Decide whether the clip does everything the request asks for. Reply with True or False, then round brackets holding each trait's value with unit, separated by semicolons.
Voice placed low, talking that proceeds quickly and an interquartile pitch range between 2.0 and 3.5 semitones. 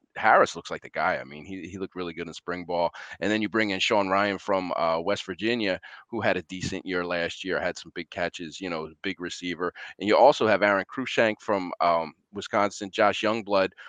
True (95 Hz; 225 wpm; 2.6 semitones)